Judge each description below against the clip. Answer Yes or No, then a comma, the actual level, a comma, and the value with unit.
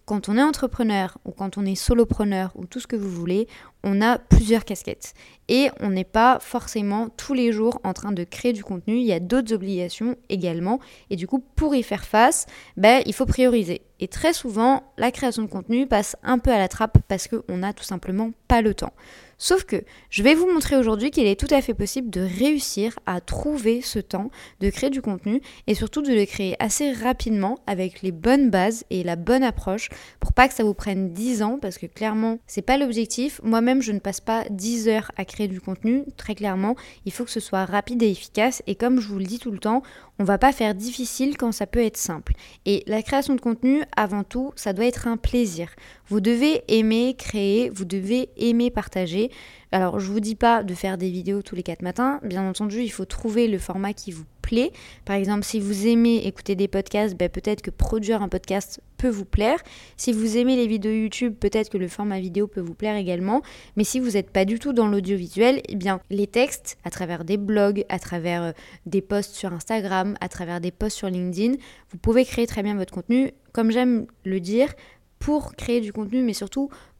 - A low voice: No, high, 215 Hz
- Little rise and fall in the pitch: No, average, 3.7 semitones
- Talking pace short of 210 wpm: No, fast, 220 wpm